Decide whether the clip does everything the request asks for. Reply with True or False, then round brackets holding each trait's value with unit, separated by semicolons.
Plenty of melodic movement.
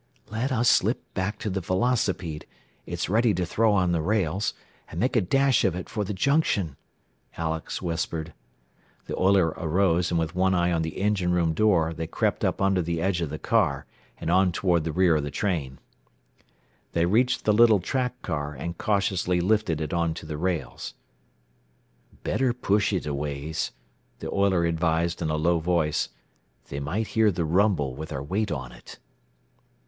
False (3.9 semitones)